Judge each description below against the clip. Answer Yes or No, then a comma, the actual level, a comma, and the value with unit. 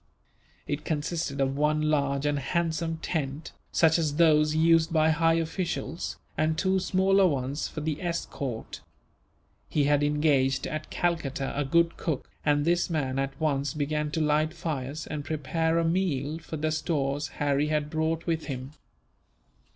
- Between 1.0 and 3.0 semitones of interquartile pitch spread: Yes, narrow, 2.4 semitones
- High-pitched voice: No, medium, 155 Hz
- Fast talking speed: No, average, 155 wpm